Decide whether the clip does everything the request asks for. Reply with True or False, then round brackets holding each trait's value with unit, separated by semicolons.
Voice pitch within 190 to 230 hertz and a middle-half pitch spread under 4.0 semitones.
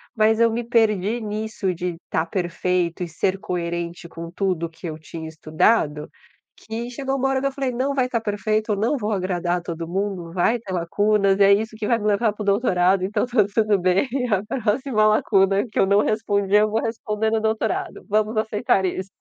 True (205 Hz; 3.5 semitones)